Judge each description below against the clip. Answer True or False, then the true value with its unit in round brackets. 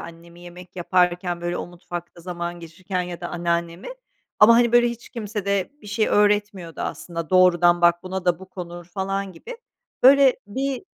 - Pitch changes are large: False (3.0 semitones)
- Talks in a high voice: False (180 Hz)